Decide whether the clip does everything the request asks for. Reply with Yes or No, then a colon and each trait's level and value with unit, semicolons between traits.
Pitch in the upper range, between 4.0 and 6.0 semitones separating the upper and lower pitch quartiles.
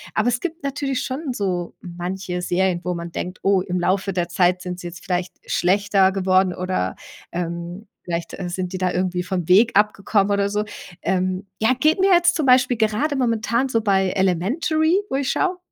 Yes: high, 195 Hz; average, 5.1 semitones